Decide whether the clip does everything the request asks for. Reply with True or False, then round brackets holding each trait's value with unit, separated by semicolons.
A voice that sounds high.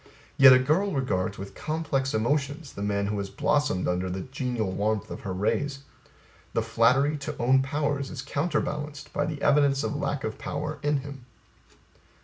False (135 Hz)